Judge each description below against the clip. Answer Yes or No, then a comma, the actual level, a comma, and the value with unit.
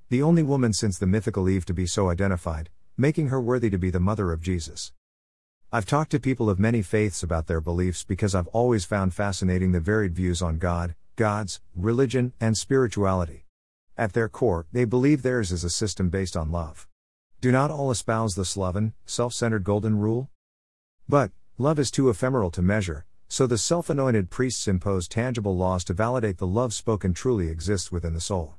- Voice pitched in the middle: No, low, 100 Hz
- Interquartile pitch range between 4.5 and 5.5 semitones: Yes, average, 4.9 semitones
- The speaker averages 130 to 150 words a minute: No, average, 190 wpm